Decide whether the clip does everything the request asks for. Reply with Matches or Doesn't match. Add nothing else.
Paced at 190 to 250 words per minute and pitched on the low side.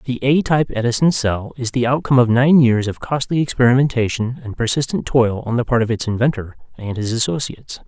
Matches